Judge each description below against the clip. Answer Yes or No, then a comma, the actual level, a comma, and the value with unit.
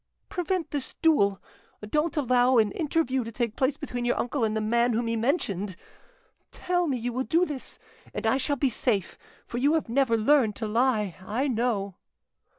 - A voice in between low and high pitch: No, high, 245 Hz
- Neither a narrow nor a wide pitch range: Yes, average, 4.5 semitones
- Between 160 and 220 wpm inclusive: Yes, average, 185 wpm